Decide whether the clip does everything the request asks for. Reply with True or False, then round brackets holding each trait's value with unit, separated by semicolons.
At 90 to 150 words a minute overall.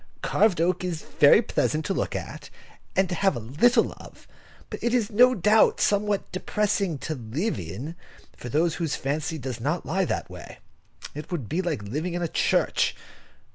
False (180 wpm)